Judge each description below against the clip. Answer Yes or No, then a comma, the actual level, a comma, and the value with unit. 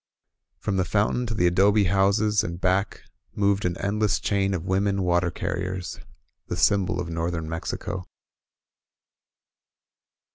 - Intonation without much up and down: Yes, narrow, 2.3 semitones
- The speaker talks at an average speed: Yes, average, 145 wpm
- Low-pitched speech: Yes, very low, 95 Hz